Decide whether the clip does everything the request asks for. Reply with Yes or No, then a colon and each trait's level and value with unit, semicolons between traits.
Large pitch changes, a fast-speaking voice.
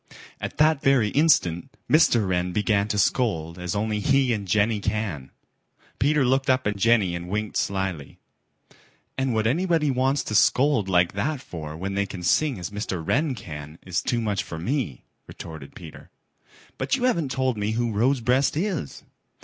No: wide, 6.5 semitones; average, 170 wpm